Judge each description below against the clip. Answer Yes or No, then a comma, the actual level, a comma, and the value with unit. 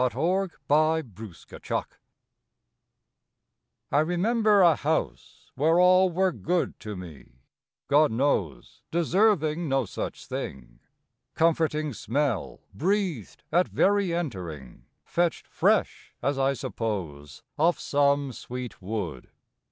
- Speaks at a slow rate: Yes, slow, 110 wpm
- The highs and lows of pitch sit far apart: Yes, wide, 8.1 semitones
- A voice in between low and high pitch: Yes, medium, 145 Hz